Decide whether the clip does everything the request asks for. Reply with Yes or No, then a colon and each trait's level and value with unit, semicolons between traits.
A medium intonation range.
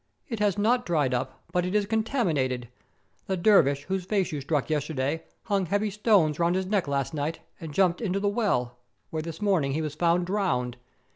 No: wide, 5.8 semitones